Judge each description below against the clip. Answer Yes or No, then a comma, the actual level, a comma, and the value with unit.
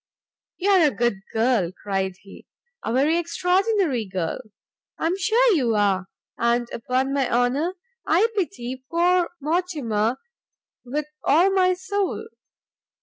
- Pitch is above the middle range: Yes, very high, 285 Hz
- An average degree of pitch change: No, wide, 7.4 semitones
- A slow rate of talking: Yes, slow, 130 wpm